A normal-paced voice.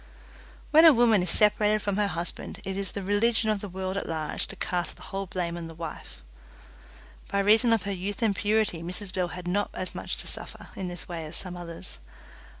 No: fast, 220 wpm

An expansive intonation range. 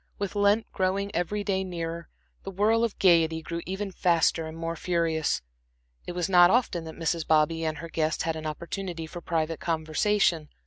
No: average, 2.9 semitones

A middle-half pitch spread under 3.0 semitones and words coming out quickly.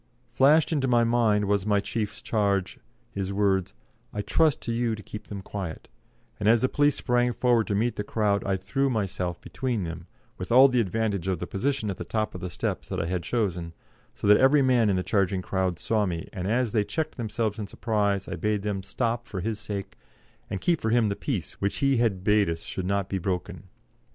No: average, 3.5 semitones; fast, 220 wpm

